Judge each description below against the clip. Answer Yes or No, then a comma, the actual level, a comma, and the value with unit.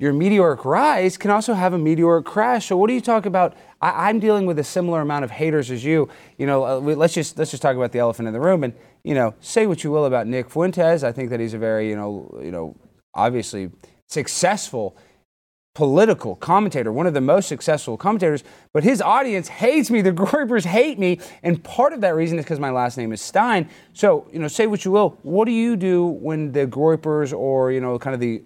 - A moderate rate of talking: No, fast, 235 wpm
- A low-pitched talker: No, medium, 160 Hz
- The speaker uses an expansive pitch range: Yes, wide, 6.5 semitones